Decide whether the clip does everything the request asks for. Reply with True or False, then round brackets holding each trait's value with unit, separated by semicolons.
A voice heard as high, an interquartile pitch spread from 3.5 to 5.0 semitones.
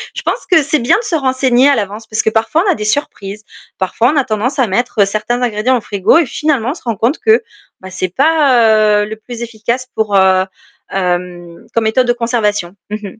True (230 Hz; 3.9 semitones)